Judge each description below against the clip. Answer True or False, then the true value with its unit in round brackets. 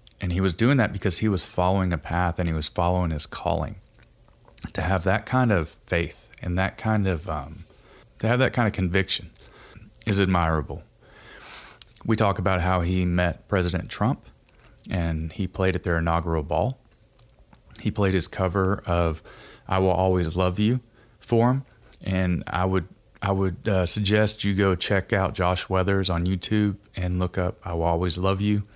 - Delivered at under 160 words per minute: False (180 wpm)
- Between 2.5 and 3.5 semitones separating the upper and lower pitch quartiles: True (3.0 semitones)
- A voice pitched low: True (95 Hz)